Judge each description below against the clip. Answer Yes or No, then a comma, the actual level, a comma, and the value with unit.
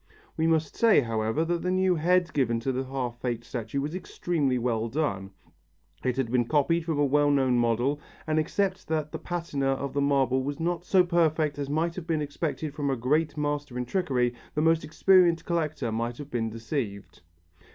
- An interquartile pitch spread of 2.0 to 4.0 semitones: No, average, 4.7 semitones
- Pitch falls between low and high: Yes, medium, 145 Hz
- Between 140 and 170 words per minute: No, average, 195 wpm